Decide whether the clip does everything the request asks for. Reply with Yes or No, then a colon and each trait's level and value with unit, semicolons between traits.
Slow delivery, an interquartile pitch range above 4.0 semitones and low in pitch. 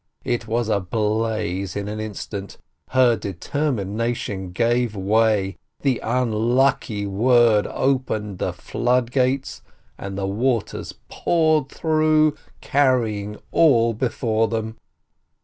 No: slow, 110 wpm; average, 3.7 semitones; low, 115 Hz